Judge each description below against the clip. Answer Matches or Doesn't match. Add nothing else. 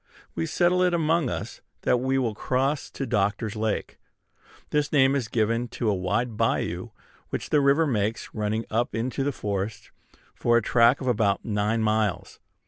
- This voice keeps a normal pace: Matches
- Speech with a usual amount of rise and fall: Matches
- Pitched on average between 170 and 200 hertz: Doesn't match